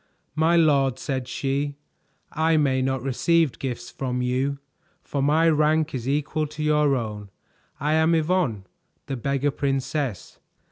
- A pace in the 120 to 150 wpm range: Yes, average, 140 wpm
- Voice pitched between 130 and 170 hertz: Yes, medium, 140 Hz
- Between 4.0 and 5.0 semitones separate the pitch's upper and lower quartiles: No, average, 2.8 semitones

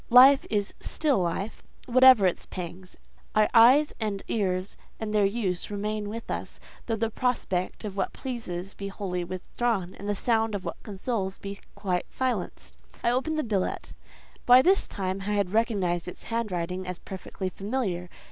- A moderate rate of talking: Yes, average, 165 wpm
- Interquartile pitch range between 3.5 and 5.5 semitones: Yes, average, 3.8 semitones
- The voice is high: Yes, high, 205 Hz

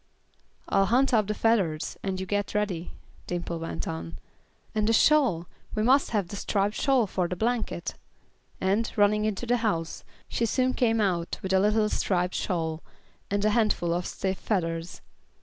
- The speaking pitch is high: Yes, high, 200 Hz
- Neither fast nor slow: Yes, average, 170 wpm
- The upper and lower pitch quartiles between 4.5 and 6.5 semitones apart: No, average, 4.0 semitones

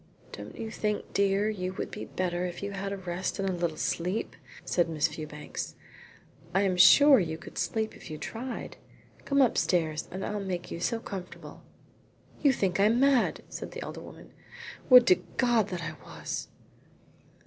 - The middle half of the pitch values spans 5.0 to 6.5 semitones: No, average, 3.9 semitones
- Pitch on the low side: No, high, 190 Hz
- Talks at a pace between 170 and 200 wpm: Yes, average, 180 wpm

